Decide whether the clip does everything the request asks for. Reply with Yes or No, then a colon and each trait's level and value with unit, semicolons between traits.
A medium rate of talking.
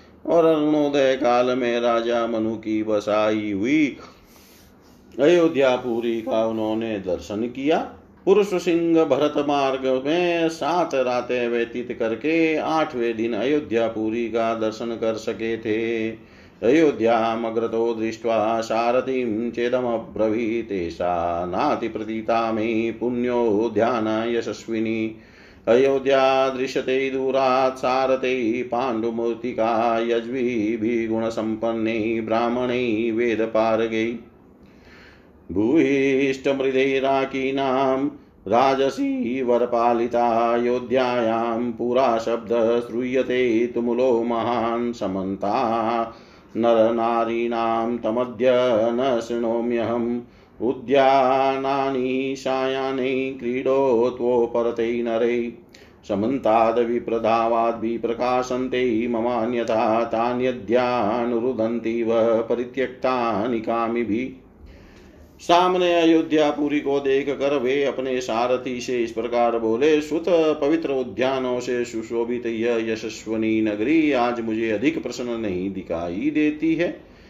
No: slow, 80 wpm